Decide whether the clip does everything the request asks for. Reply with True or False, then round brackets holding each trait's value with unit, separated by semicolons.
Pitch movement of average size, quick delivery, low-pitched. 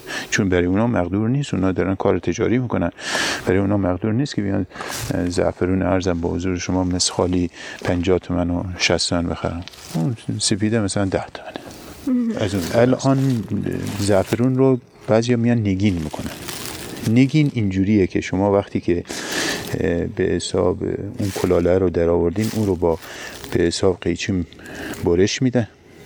False (4.4 semitones; 145 wpm; 100 Hz)